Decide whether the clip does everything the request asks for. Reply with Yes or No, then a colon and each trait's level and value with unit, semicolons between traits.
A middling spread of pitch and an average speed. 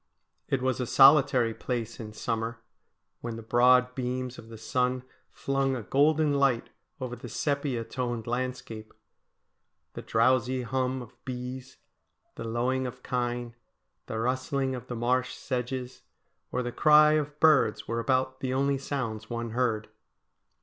No: narrow, 1.9 semitones; average, 145 wpm